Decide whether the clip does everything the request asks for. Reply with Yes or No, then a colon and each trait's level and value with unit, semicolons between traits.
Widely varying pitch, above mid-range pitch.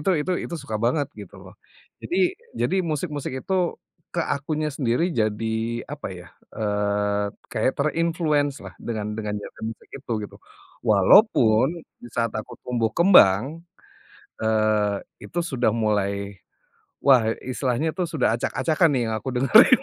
No: wide, 6.0 semitones; low, 125 Hz